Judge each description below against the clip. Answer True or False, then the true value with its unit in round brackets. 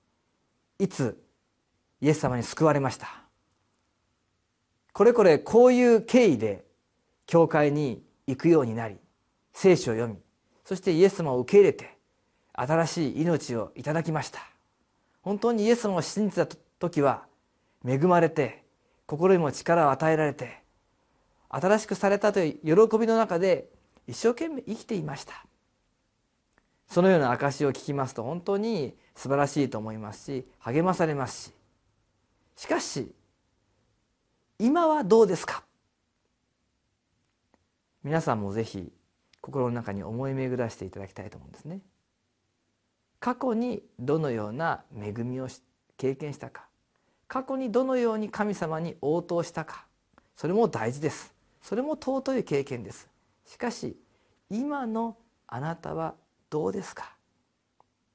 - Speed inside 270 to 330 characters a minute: False (260 characters per minute)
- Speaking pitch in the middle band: True (150 Hz)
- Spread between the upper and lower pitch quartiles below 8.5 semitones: False (9.0 semitones)